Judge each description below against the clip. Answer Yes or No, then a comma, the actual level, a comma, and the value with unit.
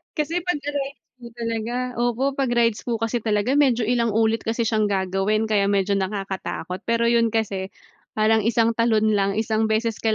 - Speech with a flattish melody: Yes, narrow, 2.1 semitones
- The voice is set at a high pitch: Yes, high, 225 Hz